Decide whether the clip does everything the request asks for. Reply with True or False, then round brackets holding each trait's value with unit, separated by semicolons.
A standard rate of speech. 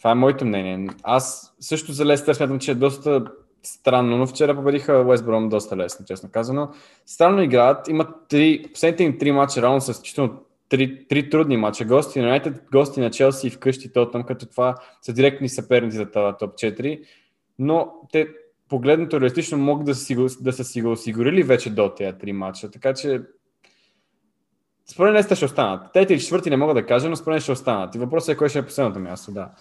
False (205 wpm)